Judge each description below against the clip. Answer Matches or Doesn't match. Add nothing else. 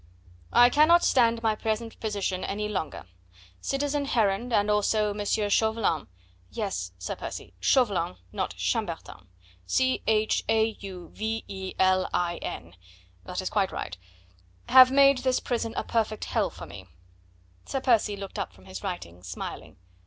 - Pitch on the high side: Matches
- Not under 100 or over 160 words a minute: Matches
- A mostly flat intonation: Doesn't match